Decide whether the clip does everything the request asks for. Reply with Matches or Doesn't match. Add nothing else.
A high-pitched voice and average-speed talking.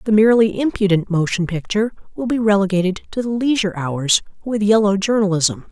Matches